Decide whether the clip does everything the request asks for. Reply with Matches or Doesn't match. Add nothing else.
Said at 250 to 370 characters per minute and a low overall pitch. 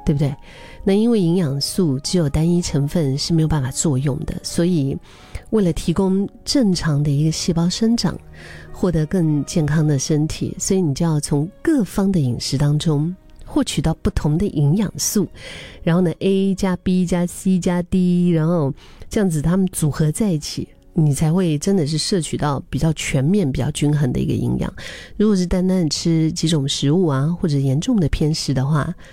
Doesn't match